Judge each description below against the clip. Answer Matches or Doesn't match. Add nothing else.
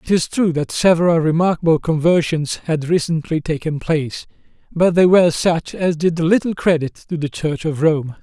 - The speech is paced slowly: Doesn't match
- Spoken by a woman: Doesn't match